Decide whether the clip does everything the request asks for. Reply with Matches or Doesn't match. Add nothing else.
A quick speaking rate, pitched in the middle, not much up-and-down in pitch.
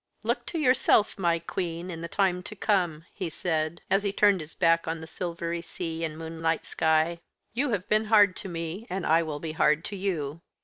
Doesn't match